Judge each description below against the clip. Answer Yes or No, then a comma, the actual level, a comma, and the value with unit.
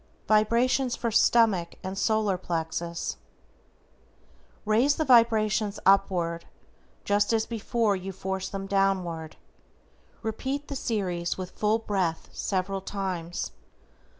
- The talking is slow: Yes, slow, 105 wpm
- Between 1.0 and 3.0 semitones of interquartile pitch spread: No, average, 3.4 semitones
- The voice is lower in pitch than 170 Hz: No, high, 200 Hz